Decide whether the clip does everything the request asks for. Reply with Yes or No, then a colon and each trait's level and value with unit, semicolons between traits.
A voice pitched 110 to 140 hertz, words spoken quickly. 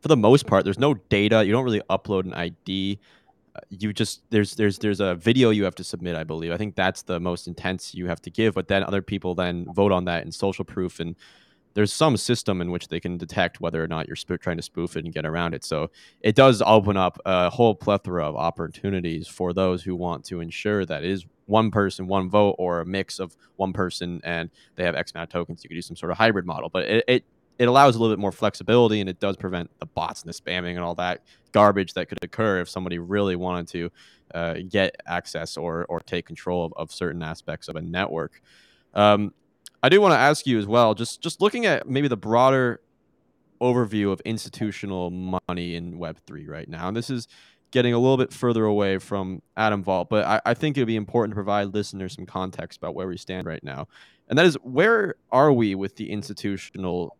No: very low, 95 Hz; fast, 235 wpm